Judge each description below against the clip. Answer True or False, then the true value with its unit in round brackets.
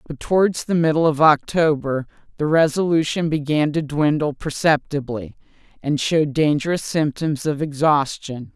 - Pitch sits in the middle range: True (150 Hz)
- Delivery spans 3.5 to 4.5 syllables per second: False (4.7 syllables/s)